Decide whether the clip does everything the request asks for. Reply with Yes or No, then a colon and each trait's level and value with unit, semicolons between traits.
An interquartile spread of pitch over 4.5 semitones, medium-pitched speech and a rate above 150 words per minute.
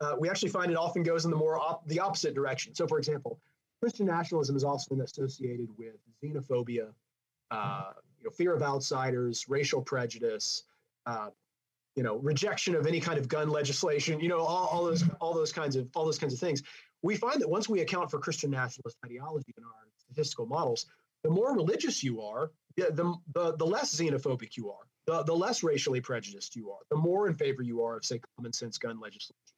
Yes: average, 4.9 semitones; medium, 150 Hz; fast, 205 wpm